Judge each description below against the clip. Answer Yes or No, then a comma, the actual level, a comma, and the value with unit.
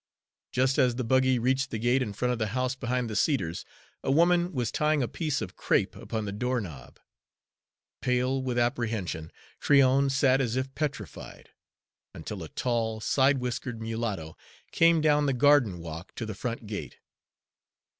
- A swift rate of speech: No, average, 165 wpm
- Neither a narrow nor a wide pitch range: Yes, average, 3.2 semitones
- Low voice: Yes, low, 125 Hz